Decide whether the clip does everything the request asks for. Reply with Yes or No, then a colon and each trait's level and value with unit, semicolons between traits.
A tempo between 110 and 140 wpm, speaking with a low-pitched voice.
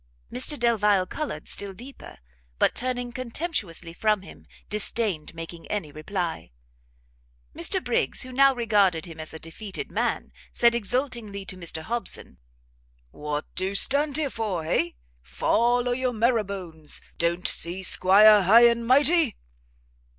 No: slow, 135 wpm; high, 210 Hz